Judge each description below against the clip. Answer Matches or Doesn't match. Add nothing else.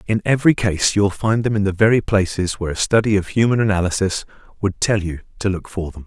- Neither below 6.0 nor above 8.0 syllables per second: Matches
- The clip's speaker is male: Matches